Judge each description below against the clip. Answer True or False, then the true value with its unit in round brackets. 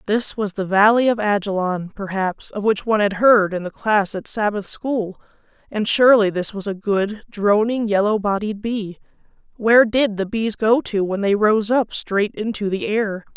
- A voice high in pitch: True (210 Hz)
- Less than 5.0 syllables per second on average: True (4.6 syllables/s)